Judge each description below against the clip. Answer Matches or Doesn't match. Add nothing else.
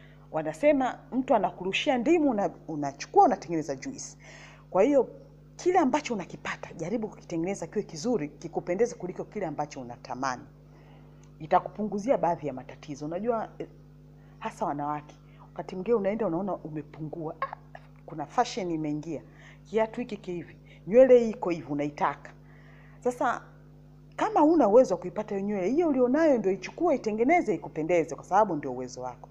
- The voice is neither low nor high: Matches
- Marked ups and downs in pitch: Matches